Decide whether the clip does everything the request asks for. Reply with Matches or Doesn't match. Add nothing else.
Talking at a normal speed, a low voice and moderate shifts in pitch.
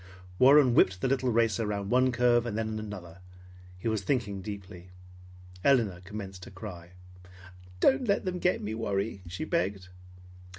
Matches